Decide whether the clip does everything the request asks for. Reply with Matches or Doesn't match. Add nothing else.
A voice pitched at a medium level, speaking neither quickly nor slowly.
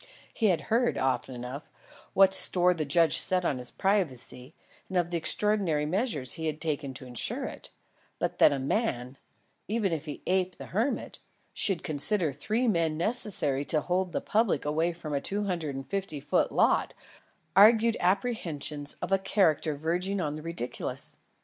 Matches